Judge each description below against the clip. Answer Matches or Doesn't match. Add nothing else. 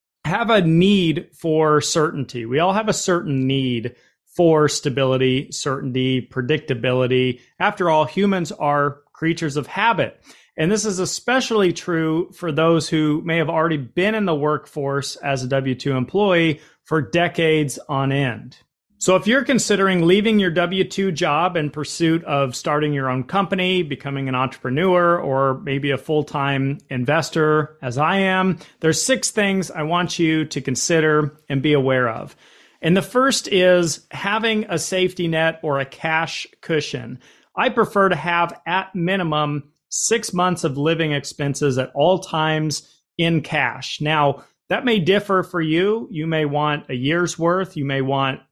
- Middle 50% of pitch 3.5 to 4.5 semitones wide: Matches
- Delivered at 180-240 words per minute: Doesn't match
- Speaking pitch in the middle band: Matches